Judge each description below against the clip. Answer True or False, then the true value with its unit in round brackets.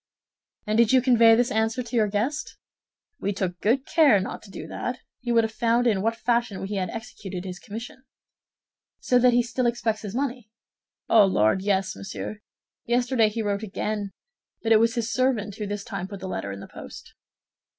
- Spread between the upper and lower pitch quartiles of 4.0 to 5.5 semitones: False (3.1 semitones)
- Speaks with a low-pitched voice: False (225 Hz)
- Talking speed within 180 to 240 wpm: True (195 wpm)